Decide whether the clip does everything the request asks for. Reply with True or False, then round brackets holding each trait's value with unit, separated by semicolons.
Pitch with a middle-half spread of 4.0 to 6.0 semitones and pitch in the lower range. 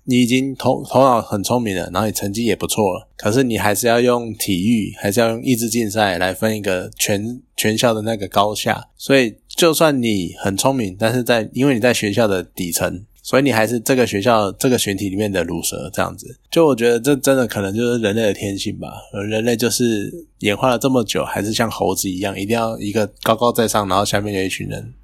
False (3.5 semitones; 110 Hz)